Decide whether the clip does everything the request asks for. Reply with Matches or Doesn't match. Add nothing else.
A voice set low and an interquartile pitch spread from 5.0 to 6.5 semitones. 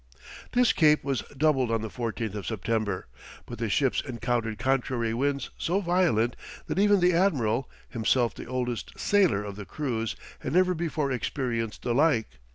Matches